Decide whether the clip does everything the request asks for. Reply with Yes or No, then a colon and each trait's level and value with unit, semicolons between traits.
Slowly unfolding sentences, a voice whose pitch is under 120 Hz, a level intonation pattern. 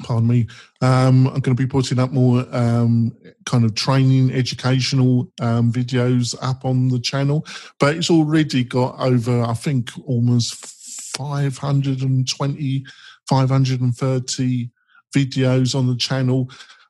No: slow, 125 wpm; low, 130 Hz; narrow, 1.6 semitones